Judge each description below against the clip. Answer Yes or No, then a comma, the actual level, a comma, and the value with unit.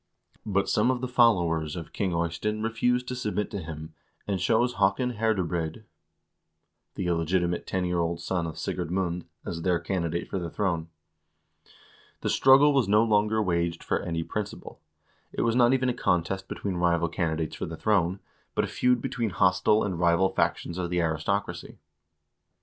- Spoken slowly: No, average, 170 wpm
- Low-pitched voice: Yes, very low, 95 Hz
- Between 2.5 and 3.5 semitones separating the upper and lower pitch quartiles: No, average, 4.2 semitones